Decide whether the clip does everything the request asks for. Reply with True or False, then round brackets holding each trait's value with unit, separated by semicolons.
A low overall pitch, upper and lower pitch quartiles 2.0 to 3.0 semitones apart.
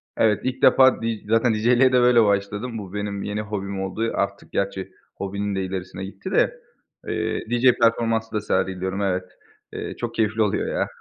True (105 Hz; 2.7 semitones)